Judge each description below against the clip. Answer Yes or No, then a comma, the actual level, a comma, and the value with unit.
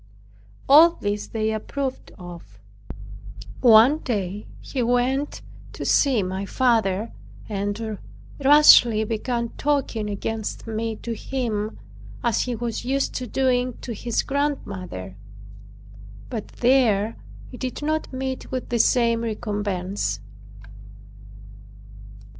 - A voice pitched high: Yes, high, 230 Hz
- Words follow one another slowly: Yes, slow, 105 wpm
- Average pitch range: Yes, average, 3.7 semitones